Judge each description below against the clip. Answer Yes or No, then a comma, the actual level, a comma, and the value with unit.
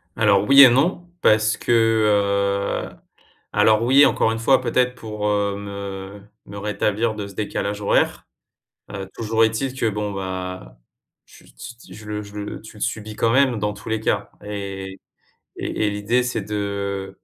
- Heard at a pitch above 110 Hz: No, low, 105 Hz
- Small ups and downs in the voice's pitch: Yes, narrow, 2.1 semitones